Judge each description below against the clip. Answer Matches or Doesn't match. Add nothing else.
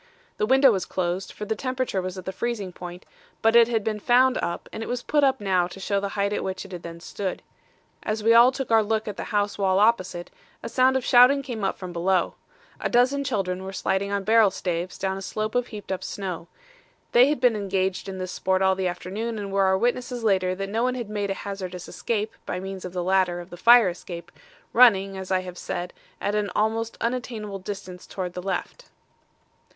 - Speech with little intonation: Doesn't match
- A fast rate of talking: Matches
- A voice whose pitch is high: Matches